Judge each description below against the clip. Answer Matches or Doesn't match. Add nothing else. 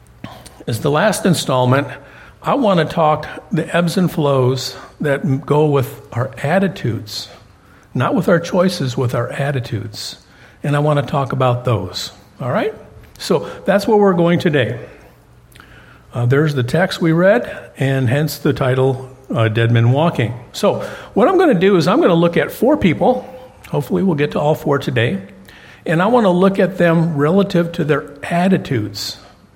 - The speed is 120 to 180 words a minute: Matches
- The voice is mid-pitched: Matches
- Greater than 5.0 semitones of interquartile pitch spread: Matches